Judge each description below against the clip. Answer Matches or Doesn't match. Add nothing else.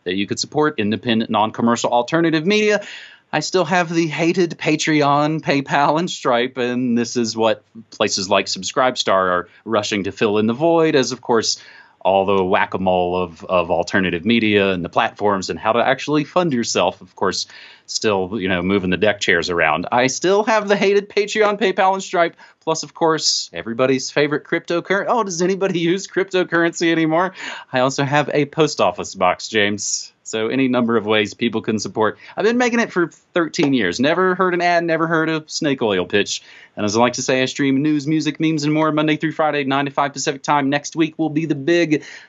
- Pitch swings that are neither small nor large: Doesn't match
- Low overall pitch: Doesn't match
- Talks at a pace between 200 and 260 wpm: Matches